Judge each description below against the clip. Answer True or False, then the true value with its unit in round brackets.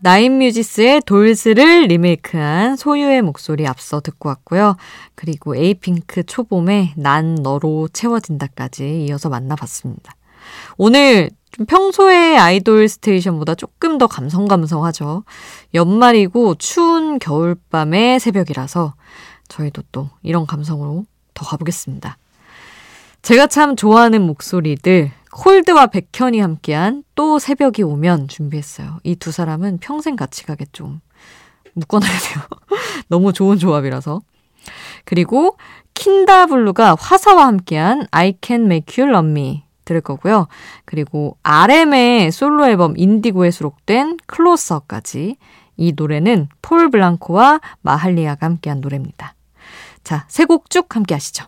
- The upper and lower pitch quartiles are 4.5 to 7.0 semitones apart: False (7.5 semitones)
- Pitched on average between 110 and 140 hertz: False (185 Hz)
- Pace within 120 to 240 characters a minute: False (300 characters per minute)